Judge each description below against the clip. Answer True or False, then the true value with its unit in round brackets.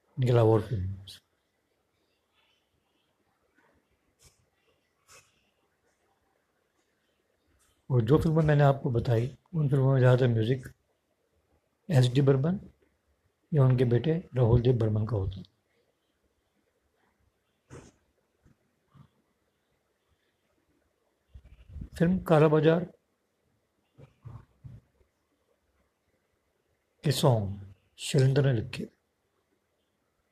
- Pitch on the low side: True (125 Hz)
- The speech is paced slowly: True (60 wpm)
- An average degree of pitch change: False (5.8 semitones)